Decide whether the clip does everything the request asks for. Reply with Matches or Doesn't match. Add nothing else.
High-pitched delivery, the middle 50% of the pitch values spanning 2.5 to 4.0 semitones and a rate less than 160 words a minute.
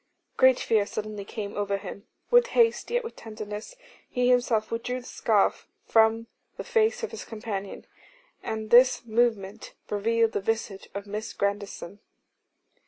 Matches